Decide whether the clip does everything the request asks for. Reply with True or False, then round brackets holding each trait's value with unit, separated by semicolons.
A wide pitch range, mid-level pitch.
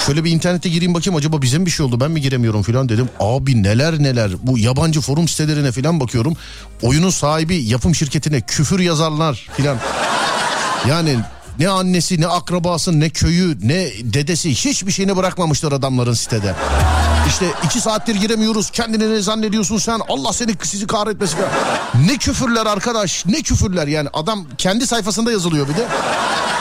True (6.3 semitones; 160 Hz)